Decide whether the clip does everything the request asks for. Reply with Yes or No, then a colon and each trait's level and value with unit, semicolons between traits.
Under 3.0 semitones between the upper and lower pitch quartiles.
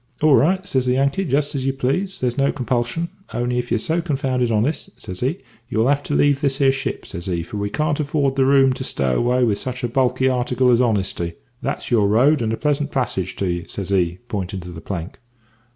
No: average, 4.5 semitones